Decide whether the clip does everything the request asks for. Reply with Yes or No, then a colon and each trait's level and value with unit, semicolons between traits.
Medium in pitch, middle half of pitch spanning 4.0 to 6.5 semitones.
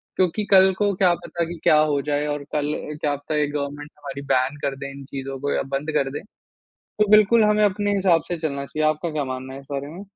Yes: medium, 150 Hz; average, 4.5 semitones